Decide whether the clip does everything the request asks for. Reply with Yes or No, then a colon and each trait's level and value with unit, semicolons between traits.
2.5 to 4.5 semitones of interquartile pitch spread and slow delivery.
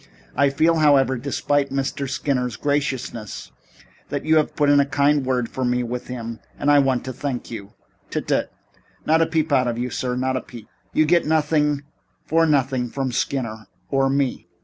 No: average, 2.8 semitones; average, 195 wpm